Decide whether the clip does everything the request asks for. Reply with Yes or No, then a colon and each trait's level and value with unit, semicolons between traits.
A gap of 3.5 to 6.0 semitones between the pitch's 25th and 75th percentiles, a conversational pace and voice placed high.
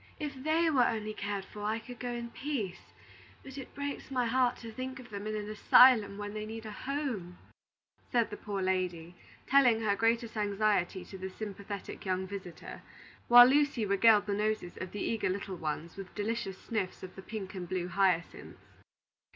Yes: average, 3.8 semitones; average, 185 wpm; high, 210 Hz